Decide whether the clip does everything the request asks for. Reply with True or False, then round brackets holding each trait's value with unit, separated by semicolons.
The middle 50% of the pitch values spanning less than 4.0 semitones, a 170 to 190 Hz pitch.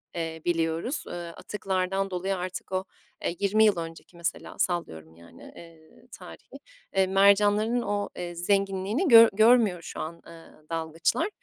True (3.4 semitones; 185 Hz)